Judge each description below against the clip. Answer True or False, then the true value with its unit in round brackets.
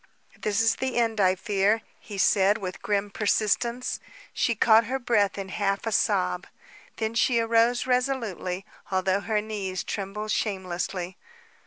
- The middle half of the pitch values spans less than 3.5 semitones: True (2.9 semitones)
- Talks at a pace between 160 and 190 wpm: False (145 wpm)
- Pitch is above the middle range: True (210 Hz)